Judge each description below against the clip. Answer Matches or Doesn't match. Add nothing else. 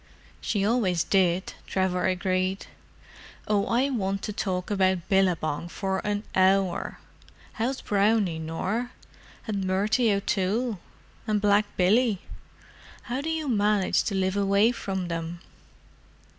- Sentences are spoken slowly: Matches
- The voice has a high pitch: Matches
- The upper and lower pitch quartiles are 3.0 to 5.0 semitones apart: Doesn't match